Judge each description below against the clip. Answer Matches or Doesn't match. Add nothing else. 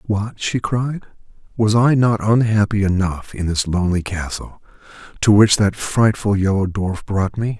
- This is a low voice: Matches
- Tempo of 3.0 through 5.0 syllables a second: Matches